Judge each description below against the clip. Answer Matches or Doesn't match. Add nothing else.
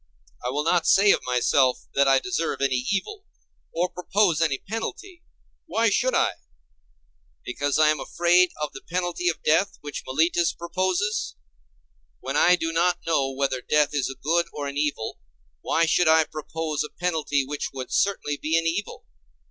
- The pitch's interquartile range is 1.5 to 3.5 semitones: Doesn't match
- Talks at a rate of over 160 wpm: Matches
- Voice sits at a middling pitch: Matches